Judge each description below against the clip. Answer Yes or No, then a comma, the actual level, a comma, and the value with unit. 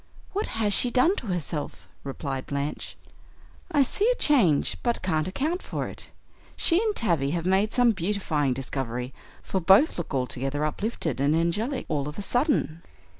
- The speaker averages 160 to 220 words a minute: Yes, average, 165 wpm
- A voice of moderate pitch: Yes, medium, 180 Hz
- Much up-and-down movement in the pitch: Yes, wide, 8.8 semitones